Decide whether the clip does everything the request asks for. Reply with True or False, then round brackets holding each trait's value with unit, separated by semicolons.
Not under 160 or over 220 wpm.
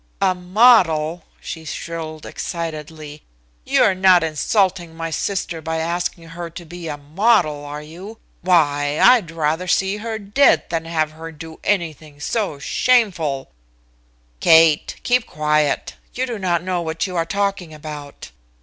False (145 wpm)